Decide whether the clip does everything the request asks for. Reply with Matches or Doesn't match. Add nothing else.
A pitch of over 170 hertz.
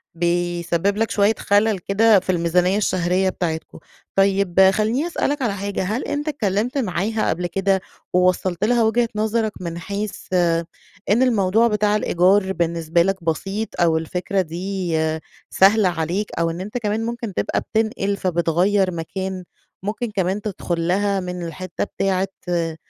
Matches